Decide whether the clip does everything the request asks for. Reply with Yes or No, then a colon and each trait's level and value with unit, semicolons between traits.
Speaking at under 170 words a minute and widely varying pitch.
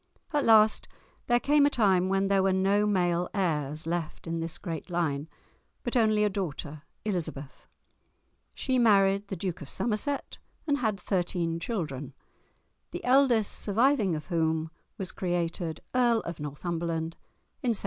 No: average, 150 wpm; average, 4.7 semitones